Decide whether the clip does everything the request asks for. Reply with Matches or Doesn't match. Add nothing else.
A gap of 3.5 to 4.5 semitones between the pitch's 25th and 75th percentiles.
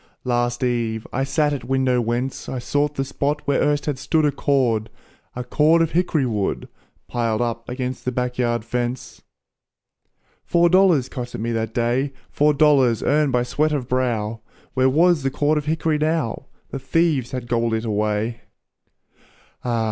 Matches